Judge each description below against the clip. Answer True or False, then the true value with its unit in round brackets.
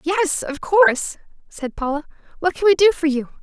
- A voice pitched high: True (330 Hz)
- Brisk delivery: False (195 wpm)